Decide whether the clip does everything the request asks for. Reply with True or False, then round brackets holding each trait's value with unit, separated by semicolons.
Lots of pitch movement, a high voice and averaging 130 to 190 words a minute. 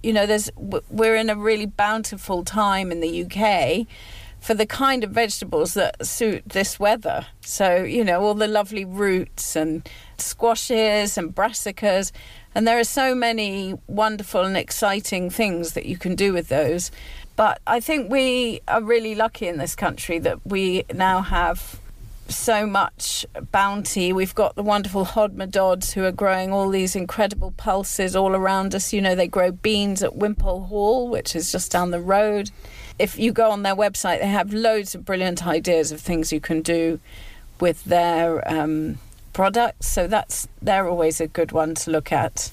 False (3.7 semitones; 195 Hz; 175 wpm)